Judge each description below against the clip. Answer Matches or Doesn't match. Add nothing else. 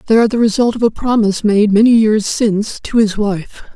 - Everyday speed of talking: Doesn't match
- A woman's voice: Matches